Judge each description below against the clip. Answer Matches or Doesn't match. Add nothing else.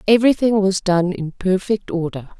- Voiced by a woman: Matches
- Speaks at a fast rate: Doesn't match